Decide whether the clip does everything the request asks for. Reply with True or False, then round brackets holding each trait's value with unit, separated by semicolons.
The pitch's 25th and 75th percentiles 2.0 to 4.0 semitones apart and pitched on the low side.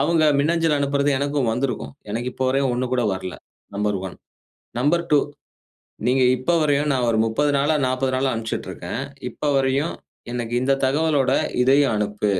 True (3.3 semitones; 130 Hz)